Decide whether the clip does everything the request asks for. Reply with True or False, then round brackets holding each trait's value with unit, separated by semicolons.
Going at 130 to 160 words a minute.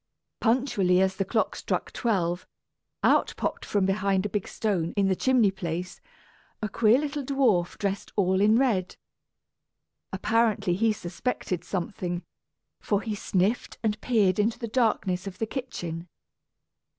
True (140 wpm)